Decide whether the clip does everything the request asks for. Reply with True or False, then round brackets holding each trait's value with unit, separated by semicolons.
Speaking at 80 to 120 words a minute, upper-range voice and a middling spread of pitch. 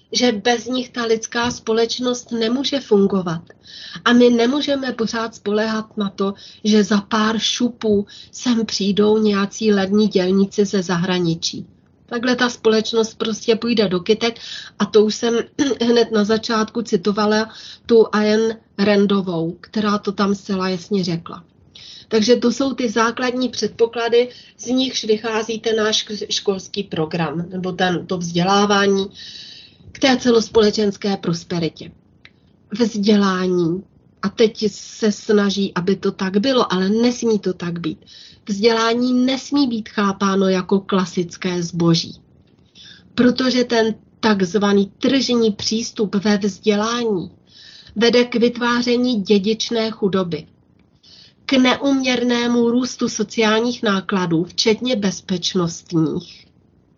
True (115 wpm; 215 Hz; 3.0 semitones)